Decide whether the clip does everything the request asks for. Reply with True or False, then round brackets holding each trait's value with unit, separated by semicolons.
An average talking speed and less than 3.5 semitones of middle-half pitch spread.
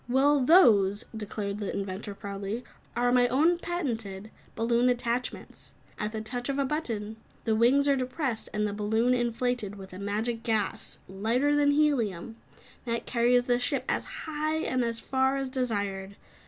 False (160 wpm; 3.9 semitones)